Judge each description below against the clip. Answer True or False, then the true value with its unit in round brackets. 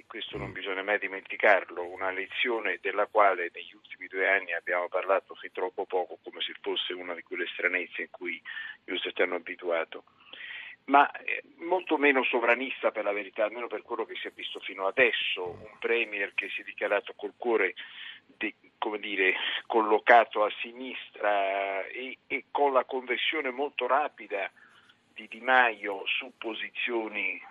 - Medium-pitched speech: False (125 Hz)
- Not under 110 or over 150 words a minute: False (160 wpm)